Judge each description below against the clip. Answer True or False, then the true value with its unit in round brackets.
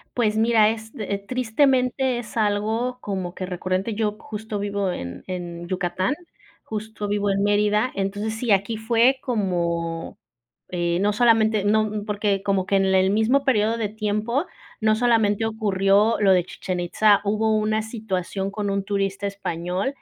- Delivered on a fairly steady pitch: True (2.3 semitones)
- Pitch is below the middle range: False (210 Hz)